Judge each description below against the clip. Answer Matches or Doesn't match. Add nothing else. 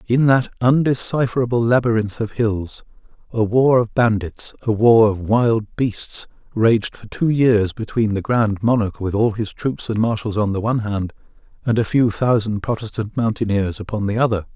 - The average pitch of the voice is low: Matches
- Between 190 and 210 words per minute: Doesn't match